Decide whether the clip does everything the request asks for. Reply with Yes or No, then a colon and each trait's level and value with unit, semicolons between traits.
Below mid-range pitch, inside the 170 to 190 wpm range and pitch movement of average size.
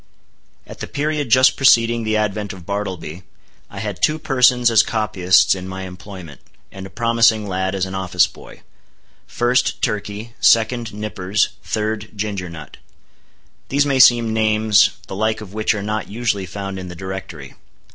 No: low, 105 Hz; average, 160 wpm; average, 3.2 semitones